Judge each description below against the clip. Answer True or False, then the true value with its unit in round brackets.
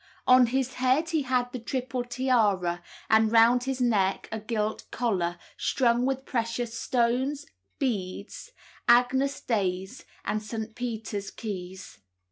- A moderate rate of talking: False (125 wpm)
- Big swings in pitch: False (3.1 semitones)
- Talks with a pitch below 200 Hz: False (235 Hz)